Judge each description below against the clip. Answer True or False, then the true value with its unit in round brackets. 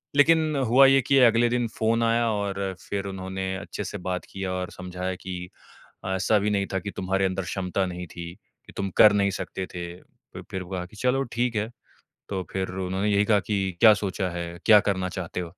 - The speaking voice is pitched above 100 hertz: False (95 Hz)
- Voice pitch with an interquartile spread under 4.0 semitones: True (2.7 semitones)